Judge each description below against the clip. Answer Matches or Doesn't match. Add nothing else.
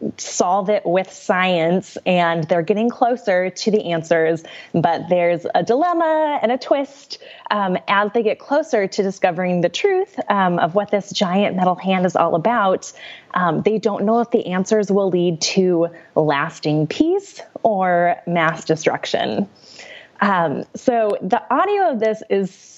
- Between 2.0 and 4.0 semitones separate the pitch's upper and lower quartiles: Doesn't match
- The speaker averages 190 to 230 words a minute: Doesn't match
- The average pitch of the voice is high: Matches